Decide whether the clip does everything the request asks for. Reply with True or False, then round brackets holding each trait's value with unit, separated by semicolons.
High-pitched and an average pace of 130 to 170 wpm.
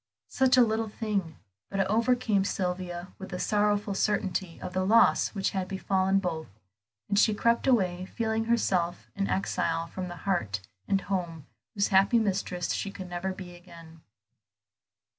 True (195 Hz; 160 wpm)